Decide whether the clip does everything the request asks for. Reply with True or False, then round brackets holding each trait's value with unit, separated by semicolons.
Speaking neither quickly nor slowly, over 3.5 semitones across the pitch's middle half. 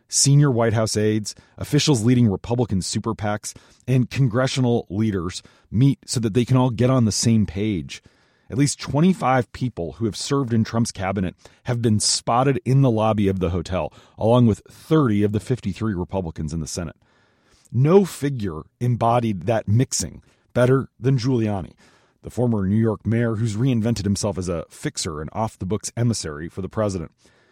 True (170 wpm; 4.1 semitones)